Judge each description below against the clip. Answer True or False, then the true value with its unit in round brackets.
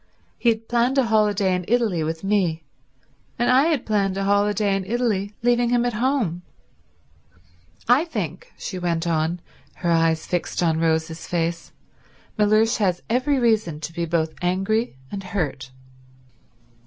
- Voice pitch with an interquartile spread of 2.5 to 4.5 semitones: False (5.4 semitones)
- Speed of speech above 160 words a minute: False (150 wpm)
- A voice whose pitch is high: True (195 Hz)